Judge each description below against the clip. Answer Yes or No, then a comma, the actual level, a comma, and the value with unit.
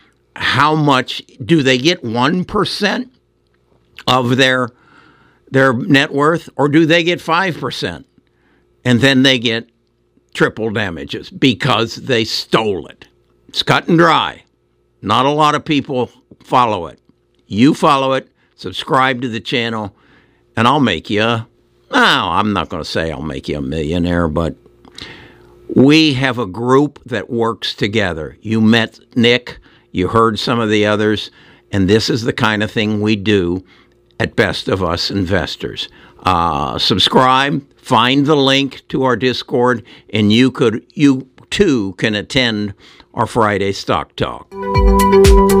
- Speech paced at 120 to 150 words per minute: Yes, average, 145 wpm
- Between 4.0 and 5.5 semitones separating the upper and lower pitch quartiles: Yes, average, 5.2 semitones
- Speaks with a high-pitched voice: No, low, 120 Hz